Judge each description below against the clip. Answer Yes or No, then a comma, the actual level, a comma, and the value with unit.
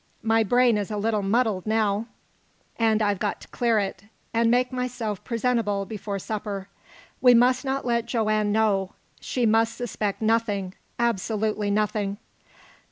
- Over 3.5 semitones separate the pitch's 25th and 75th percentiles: No, narrow, 2.4 semitones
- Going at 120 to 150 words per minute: Yes, average, 145 wpm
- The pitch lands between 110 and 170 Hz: No, high, 220 Hz